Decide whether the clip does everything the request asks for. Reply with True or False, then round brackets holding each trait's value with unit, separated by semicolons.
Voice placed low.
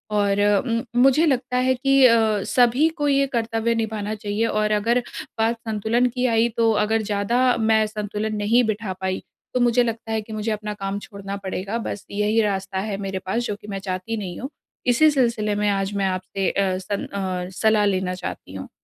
False (215 Hz)